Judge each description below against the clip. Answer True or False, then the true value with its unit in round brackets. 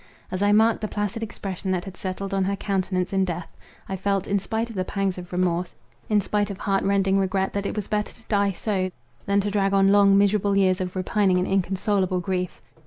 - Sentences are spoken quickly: True (225 wpm)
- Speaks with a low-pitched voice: False (195 Hz)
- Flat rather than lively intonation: True (1.5 semitones)